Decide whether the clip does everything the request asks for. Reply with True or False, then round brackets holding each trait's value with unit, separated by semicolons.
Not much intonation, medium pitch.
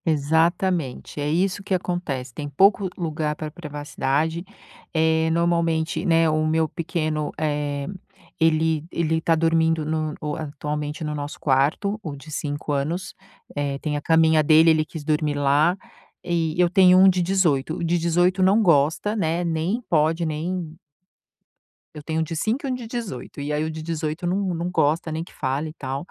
True (2.3 semitones; 160 Hz)